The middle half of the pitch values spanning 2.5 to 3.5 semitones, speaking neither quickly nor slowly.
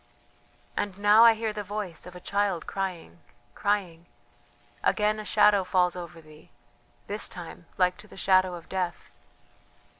Yes: average, 2.8 semitones; average, 150 wpm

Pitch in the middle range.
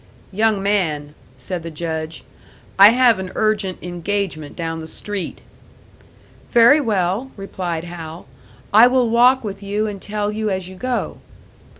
No: high, 195 Hz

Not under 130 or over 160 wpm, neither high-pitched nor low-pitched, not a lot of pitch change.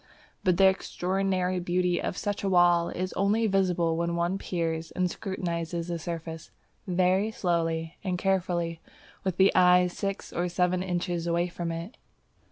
Yes: average, 155 wpm; medium, 180 Hz; narrow, 1.7 semitones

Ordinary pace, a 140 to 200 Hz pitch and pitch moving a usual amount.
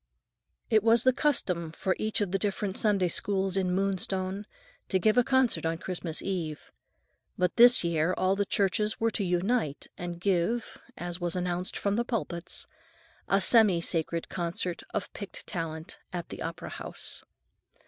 Yes: average, 160 wpm; high, 190 Hz; average, 3.3 semitones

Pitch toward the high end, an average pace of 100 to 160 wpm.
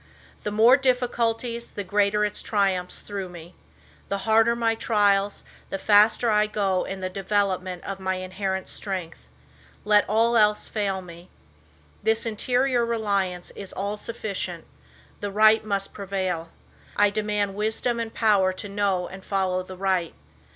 Yes: high, 205 Hz; average, 150 wpm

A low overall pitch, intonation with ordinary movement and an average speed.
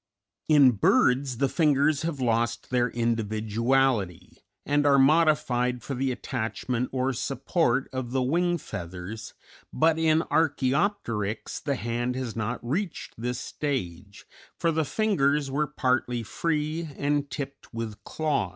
No: low, 130 Hz; average, 4.1 semitones; slow, 130 wpm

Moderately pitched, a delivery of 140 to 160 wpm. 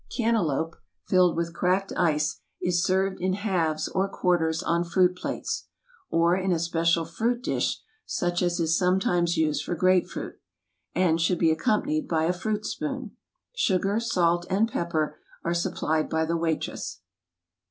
Yes: medium, 175 Hz; average, 155 wpm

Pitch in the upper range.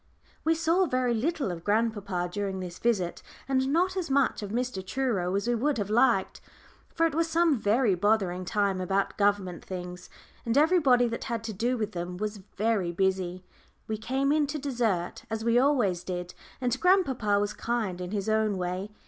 Yes: high, 220 Hz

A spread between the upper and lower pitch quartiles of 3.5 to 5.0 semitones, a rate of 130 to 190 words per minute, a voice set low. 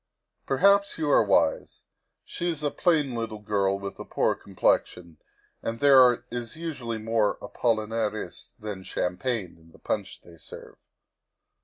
No: wide, 5.4 semitones; average, 140 wpm; low, 115 Hz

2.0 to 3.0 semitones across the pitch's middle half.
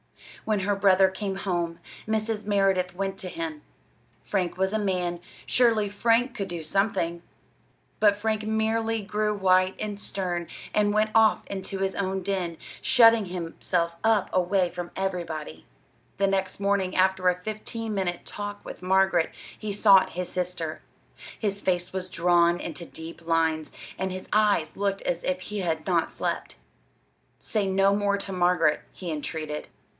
Yes: narrow, 2.6 semitones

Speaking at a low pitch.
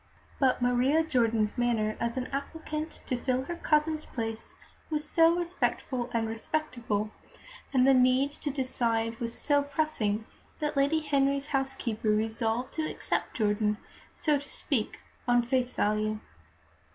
No: very high, 255 Hz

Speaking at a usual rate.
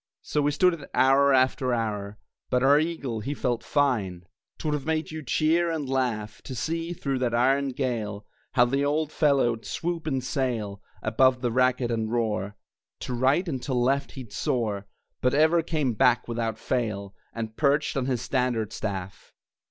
Yes: average, 175 wpm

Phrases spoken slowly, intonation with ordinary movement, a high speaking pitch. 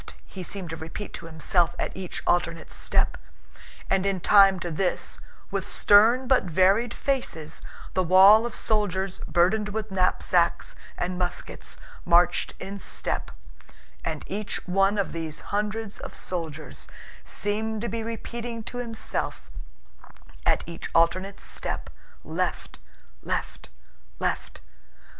Yes: slow, 125 wpm; average, 3.5 semitones; high, 195 Hz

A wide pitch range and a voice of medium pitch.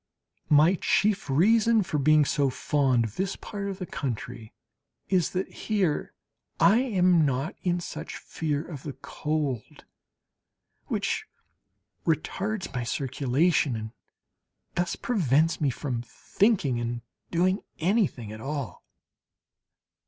Yes: wide, 5.9 semitones; medium, 155 Hz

